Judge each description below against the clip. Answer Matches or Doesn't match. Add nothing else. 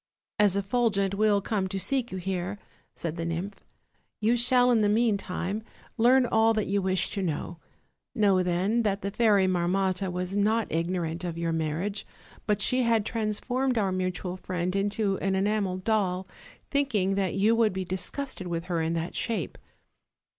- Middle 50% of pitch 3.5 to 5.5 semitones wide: Doesn't match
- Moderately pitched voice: Doesn't match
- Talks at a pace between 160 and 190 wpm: Matches